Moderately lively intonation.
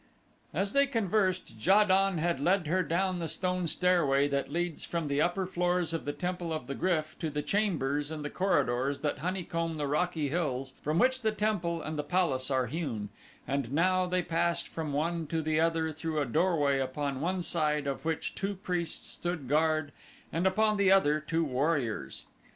Yes: average, 3.8 semitones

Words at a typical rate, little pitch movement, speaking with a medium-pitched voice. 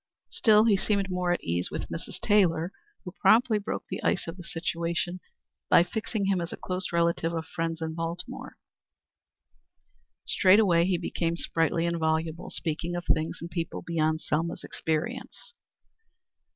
Yes: average, 155 wpm; narrow, 2.1 semitones; medium, 170 Hz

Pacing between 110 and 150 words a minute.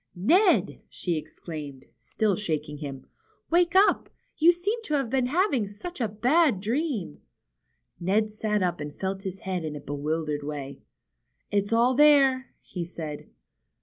Yes: average, 145 wpm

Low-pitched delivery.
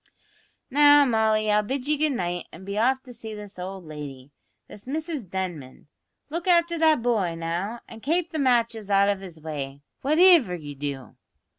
No: high, 215 Hz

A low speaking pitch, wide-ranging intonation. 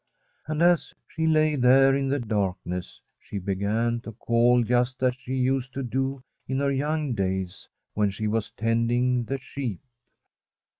No: low, 125 Hz; average, 3.8 semitones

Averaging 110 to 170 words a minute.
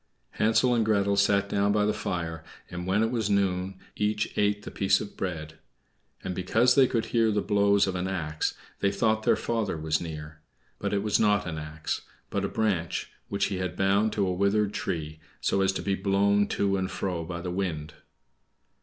No: average, 200 wpm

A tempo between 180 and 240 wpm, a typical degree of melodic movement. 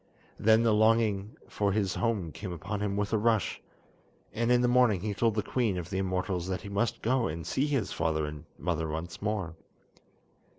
Yes: average, 200 wpm; average, 4.1 semitones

